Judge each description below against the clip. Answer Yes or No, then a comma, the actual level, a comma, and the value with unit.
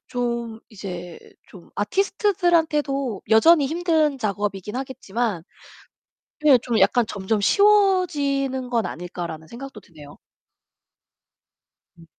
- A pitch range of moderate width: No, wide, 6.9 semitones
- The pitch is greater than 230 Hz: Yes, high, 245 Hz